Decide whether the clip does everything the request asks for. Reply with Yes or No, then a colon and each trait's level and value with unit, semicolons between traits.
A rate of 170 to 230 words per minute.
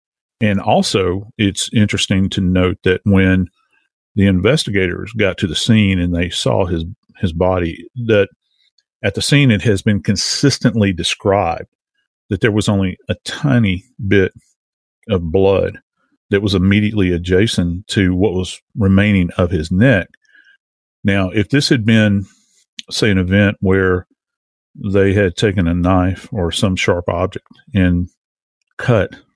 No: average, 140 wpm